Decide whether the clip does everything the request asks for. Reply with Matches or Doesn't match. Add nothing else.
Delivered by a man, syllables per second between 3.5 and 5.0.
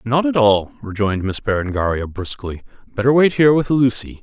Doesn't match